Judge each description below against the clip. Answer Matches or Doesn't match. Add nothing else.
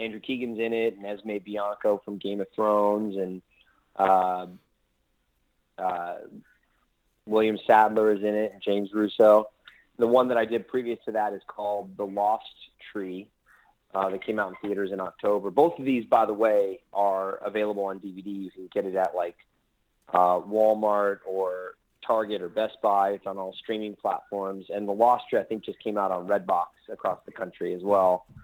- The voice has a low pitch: Matches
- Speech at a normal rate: Matches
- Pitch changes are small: Matches